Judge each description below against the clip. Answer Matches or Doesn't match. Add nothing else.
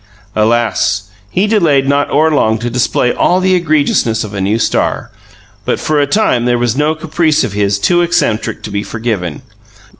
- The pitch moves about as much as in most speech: Doesn't match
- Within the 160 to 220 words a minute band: Matches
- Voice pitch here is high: Doesn't match